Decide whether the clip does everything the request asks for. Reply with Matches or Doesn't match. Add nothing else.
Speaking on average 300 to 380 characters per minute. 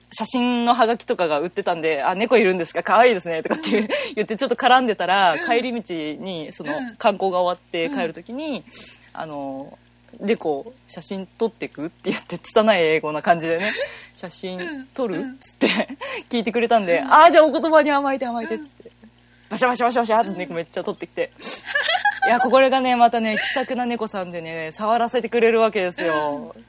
Doesn't match